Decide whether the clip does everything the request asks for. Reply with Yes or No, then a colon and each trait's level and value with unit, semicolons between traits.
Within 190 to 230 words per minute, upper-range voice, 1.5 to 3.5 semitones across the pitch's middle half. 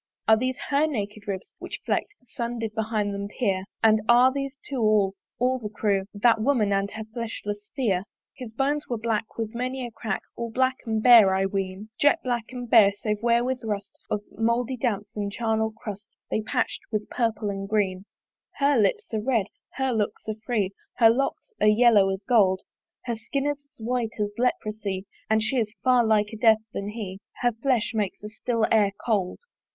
Yes: average, 200 wpm; high, 220 Hz; average, 2.8 semitones